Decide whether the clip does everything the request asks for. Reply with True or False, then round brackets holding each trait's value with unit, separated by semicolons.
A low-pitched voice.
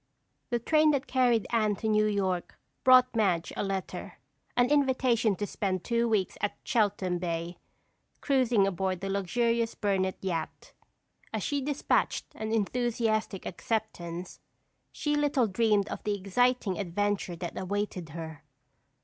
False (210 Hz)